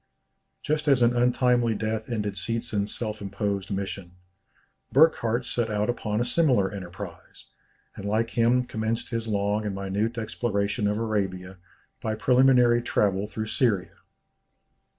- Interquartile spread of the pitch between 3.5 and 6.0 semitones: No, average, 3.0 semitones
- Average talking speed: No, slow, 130 wpm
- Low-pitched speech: Yes, low, 110 Hz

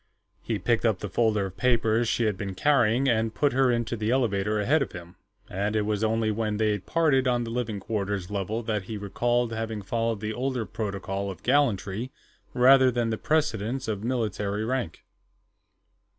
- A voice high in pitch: No, low, 110 Hz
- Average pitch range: Yes, average, 3.0 semitones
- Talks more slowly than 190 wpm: Yes, average, 180 wpm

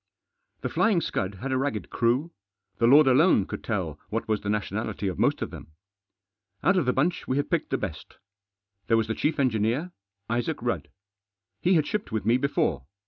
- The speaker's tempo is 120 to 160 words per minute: No, average, 195 wpm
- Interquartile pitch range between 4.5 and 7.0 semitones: Yes, average, 5.3 semitones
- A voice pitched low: Yes, low, 120 Hz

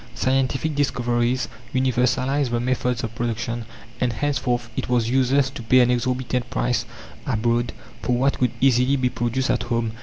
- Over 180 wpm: No, average, 155 wpm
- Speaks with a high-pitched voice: No, low, 125 Hz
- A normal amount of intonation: No, narrow, 1.6 semitones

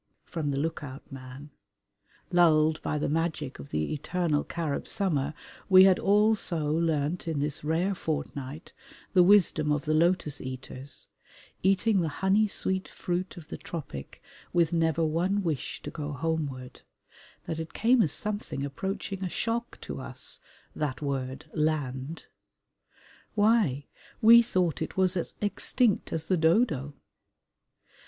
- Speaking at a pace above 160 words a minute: No, average, 145 wpm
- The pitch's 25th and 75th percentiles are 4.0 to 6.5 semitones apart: Yes, average, 4.4 semitones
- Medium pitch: Yes, medium, 160 Hz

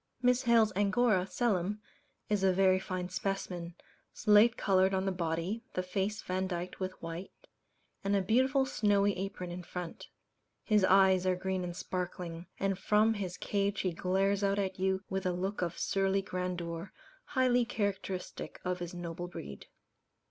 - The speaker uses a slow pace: No, average, 155 wpm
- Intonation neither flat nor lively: No, narrow, 2.0 semitones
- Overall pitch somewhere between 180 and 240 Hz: Yes, high, 190 Hz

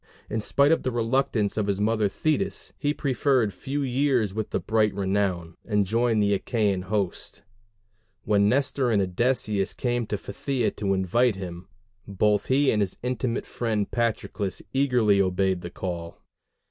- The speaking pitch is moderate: No, low, 105 Hz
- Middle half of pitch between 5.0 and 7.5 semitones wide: No, average, 4.1 semitones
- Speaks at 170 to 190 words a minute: No, average, 150 wpm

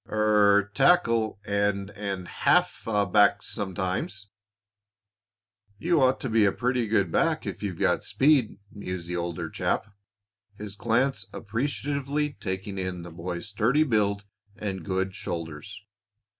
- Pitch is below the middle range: Yes, low, 105 Hz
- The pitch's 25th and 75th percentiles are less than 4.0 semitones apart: Yes, average, 3.6 semitones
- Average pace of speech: No, slow, 130 wpm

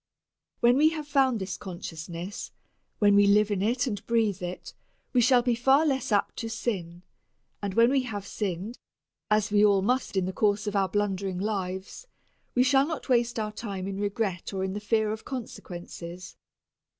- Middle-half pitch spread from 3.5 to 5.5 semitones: Yes, average, 3.9 semitones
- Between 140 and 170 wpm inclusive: No, average, 180 wpm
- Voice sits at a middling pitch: No, high, 210 Hz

